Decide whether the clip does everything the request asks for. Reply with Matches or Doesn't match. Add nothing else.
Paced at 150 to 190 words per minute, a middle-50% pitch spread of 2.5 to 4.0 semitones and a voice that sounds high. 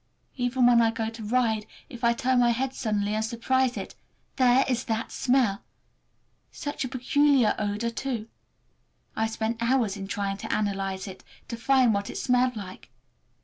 Matches